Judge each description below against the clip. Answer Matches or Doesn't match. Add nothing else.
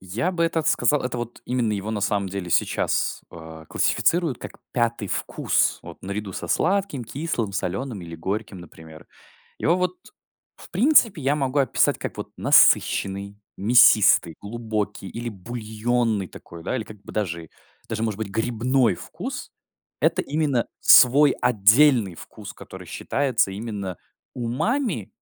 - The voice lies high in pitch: Doesn't match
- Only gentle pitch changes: Doesn't match